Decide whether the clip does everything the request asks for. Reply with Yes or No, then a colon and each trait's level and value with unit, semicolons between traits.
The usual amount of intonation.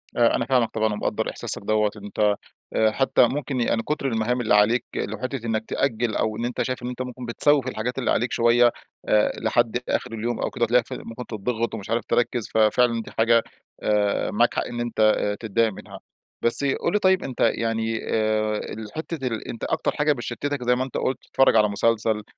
No: narrow, 2.2 semitones